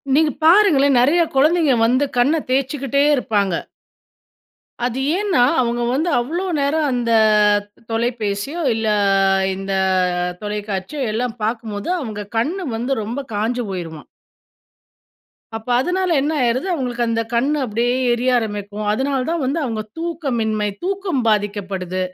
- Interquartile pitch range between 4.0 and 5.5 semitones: Yes, average, 4.8 semitones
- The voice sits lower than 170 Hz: No, high, 245 Hz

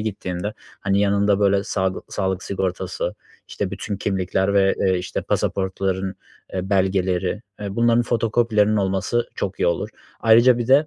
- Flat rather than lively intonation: Yes, narrow, 2.1 semitones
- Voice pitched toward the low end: Yes, low, 100 Hz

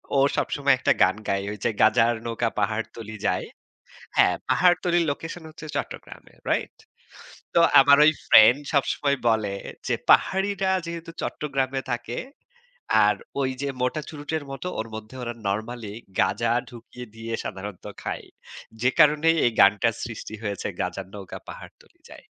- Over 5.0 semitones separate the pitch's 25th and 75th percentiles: Yes, wide, 5.4 semitones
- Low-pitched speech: Yes, low, 120 Hz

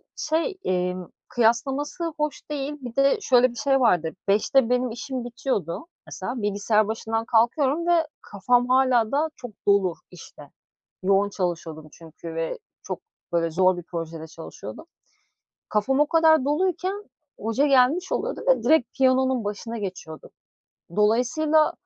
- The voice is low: No, high, 240 Hz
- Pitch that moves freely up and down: Yes, wide, 6.0 semitones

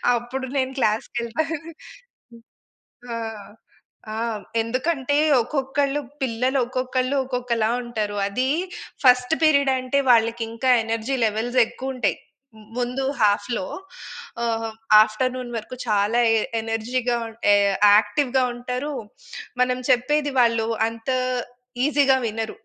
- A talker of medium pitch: No, high, 245 Hz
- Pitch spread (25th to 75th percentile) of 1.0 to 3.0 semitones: Yes, average, 2.7 semitones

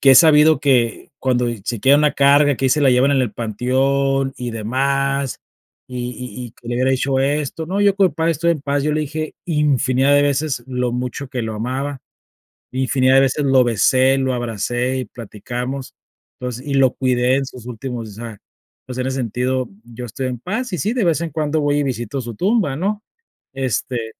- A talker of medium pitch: No, low, 130 Hz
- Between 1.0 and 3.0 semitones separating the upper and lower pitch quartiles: Yes, narrow, 2.6 semitones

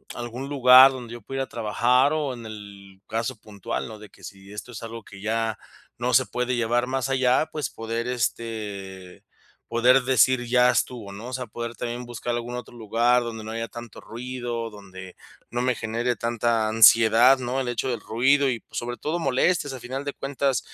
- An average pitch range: No, narrow, 2.2 semitones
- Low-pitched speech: Yes, low, 120 Hz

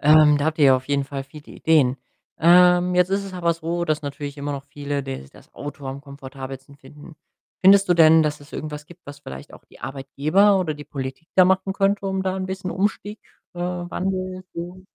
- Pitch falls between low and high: Yes, medium, 155 Hz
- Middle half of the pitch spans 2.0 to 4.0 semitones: No, average, 4.5 semitones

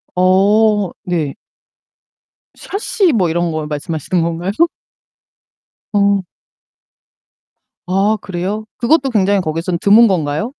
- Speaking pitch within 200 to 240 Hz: No, high, 190 Hz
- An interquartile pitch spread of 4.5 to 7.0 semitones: No, average, 3.8 semitones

